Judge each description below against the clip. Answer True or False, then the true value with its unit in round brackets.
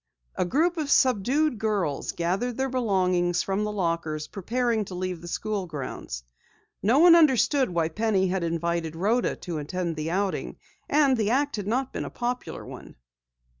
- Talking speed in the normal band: True (170 wpm)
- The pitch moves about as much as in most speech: False (6.4 semitones)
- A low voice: False (200 Hz)